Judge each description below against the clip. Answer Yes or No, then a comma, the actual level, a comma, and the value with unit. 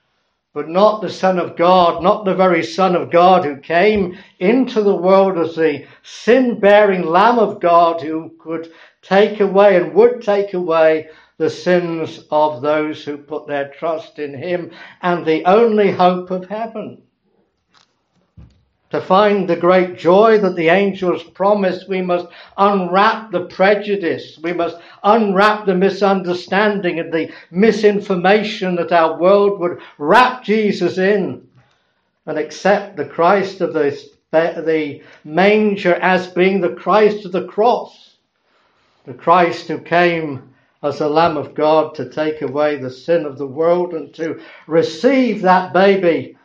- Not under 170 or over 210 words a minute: No, average, 145 wpm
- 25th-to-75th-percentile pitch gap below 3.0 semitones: No, average, 3.6 semitones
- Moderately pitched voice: Yes, medium, 175 Hz